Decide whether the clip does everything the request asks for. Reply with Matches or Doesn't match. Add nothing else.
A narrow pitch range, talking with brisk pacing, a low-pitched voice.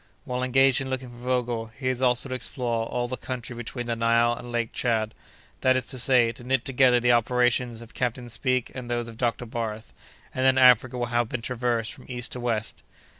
Matches